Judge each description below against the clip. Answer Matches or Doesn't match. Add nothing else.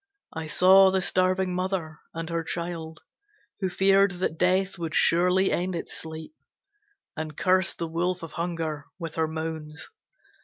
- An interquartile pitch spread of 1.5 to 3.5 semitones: Matches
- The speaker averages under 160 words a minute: Matches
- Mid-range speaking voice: Matches